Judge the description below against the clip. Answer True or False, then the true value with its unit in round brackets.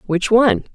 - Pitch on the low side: False (220 Hz)